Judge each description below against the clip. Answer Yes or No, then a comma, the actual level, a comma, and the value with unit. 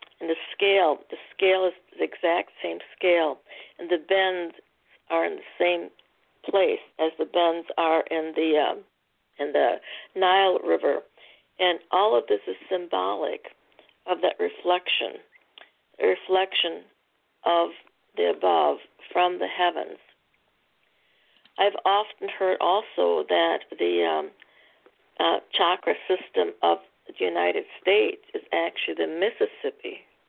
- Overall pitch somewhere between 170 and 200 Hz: Yes, medium, 185 Hz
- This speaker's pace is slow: Yes, slow, 125 wpm